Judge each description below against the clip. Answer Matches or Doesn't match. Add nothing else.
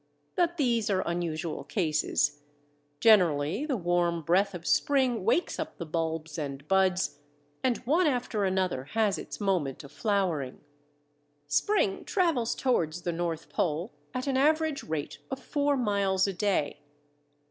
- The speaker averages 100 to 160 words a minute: Matches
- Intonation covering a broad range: Matches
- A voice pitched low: Doesn't match